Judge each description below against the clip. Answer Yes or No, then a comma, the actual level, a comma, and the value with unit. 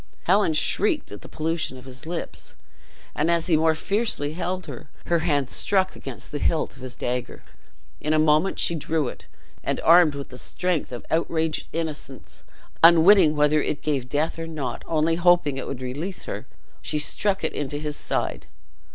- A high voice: No, medium, 155 Hz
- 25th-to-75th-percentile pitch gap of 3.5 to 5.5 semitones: No, average, 2.9 semitones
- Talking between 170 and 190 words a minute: Yes, average, 180 wpm